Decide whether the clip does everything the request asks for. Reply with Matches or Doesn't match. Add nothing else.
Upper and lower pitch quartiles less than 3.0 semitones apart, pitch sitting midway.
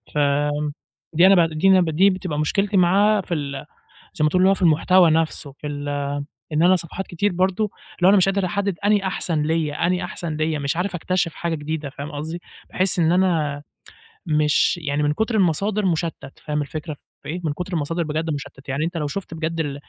Doesn't match